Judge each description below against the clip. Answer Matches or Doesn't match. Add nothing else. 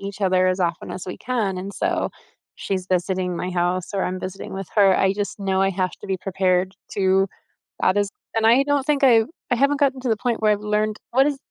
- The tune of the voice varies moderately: Matches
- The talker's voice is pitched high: Matches